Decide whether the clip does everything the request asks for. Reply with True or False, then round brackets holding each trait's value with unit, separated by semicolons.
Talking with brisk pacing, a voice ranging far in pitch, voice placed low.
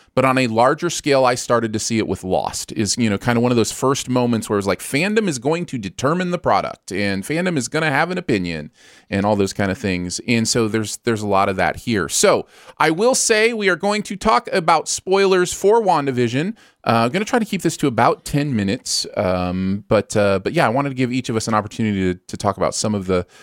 True (260 wpm; 7.6 semitones; 120 Hz)